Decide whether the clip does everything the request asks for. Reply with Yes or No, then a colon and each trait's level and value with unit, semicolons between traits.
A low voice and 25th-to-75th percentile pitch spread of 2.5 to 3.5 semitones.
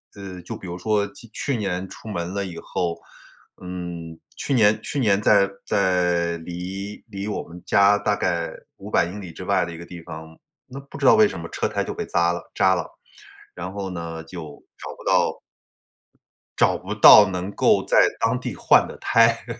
Yes: very low, 95 Hz; average, 3.1 semitones